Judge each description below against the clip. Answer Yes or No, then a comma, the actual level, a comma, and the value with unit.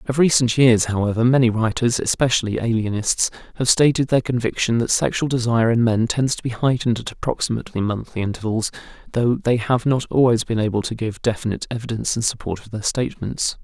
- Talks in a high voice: No, low, 120 Hz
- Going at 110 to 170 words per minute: No, average, 180 wpm